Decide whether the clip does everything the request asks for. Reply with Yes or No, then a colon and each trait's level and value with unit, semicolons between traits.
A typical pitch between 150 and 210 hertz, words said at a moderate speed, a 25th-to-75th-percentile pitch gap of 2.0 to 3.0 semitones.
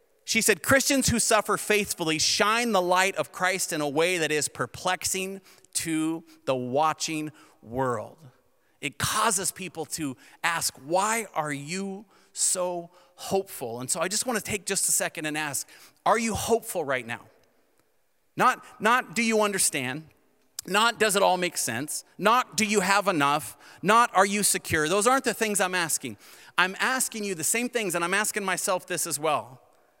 No: medium, 185 Hz; average, 175 wpm; average, 5.1 semitones